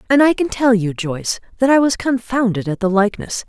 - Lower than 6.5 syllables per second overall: Yes, 5.9 syllables/s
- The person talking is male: No, female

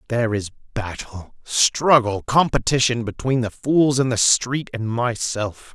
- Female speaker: No, male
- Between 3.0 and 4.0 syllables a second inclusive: Yes, 3.9 syllables/s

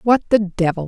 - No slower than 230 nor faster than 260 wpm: No, fast, 205 wpm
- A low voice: No, high, 200 Hz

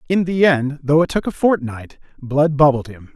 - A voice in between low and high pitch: Yes, medium, 145 Hz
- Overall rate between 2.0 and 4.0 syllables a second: No, 4.7 syllables/s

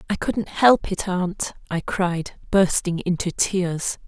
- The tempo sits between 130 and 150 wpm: Yes, average, 145 wpm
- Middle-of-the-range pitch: Yes, medium, 180 Hz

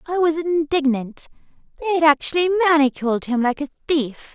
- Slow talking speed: No, average, 150 wpm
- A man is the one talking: No, female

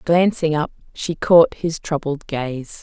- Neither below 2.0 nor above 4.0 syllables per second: Yes, 3.6 syllables/s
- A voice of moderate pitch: Yes, medium, 155 Hz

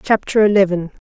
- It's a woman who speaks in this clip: Yes, female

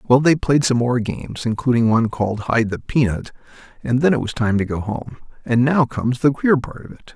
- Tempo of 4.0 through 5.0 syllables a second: No, 5.7 syllables/s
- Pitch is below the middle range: Yes, low, 125 Hz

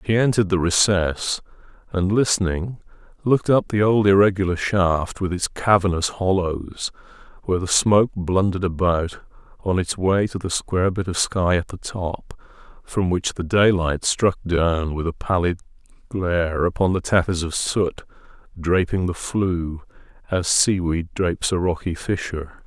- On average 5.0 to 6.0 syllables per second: No, 4.6 syllables/s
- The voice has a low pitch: Yes, very low, 90 Hz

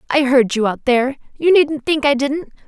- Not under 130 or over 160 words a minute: No, average, 200 wpm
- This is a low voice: No, very high, 275 Hz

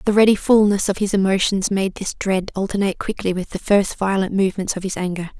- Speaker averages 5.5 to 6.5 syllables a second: Yes, 6.0 syllables/s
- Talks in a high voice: Yes, high, 195 Hz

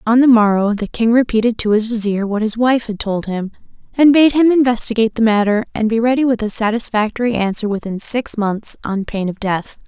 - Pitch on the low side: No, high, 225 Hz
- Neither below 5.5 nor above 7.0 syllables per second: Yes, 5.6 syllables/s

